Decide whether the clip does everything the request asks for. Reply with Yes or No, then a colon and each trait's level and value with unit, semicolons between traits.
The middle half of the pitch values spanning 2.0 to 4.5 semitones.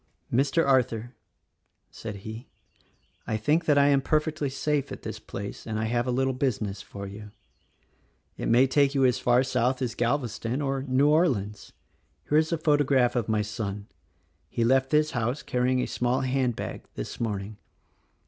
Yes: average, 3.8 semitones